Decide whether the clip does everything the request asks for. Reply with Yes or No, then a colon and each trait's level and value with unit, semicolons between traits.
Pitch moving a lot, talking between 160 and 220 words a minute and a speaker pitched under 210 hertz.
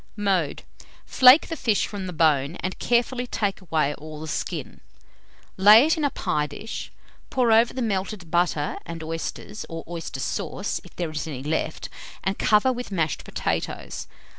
Yes: wide, 6.1 semitones; average, 165 wpm; medium, 185 Hz